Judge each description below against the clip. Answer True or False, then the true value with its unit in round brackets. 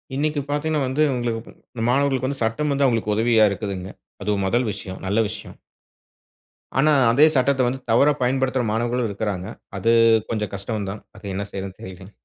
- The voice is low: True (115 Hz)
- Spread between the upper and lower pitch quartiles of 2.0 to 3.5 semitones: False (4.5 semitones)